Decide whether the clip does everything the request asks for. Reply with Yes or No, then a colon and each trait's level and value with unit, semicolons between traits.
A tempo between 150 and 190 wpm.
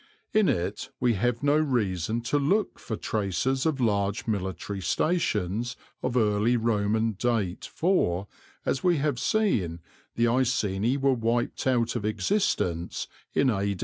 No: average, 140 wpm